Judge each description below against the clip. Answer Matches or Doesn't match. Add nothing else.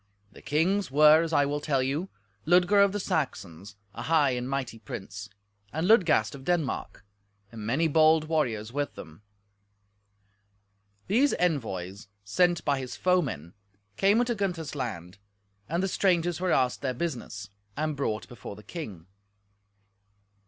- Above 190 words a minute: Doesn't match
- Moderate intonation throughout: Doesn't match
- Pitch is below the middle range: Doesn't match